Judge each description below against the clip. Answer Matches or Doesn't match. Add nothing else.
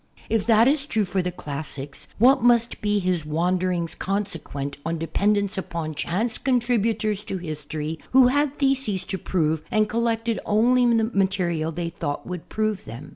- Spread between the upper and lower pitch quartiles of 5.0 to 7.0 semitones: Matches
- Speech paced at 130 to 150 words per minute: Doesn't match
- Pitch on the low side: Doesn't match